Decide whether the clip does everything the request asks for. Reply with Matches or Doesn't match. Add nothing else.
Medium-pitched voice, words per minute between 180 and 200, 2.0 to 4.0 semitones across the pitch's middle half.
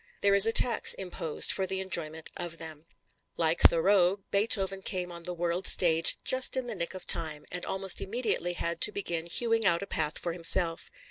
Matches